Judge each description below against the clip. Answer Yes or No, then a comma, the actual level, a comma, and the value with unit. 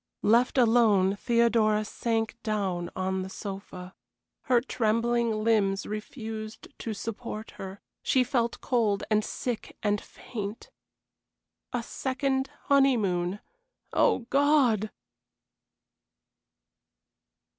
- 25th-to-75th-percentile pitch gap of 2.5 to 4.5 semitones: Yes, average, 3.0 semitones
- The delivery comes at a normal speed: No, slow, 90 wpm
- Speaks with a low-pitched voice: No, high, 220 Hz